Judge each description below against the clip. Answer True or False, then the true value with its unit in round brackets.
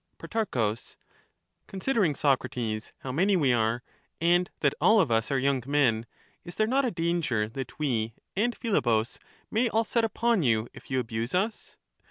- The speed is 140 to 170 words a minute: False (190 wpm)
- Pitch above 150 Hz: False (140 Hz)